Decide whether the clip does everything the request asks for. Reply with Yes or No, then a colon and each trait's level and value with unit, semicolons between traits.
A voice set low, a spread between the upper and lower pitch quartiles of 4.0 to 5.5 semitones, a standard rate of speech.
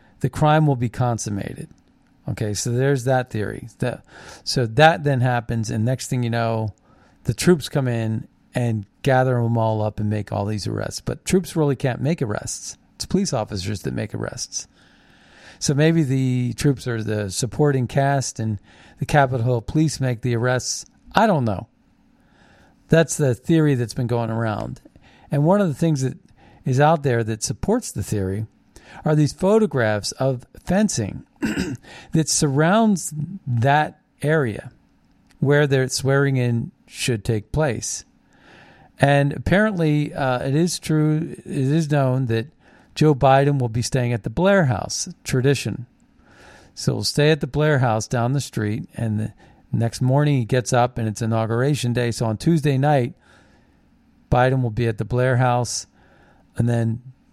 Yes: low, 130 Hz; average, 4.5 semitones; average, 160 wpm